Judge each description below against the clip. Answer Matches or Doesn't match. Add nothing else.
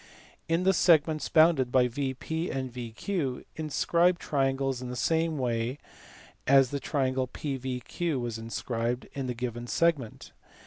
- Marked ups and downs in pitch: Doesn't match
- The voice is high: Doesn't match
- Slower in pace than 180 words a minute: Matches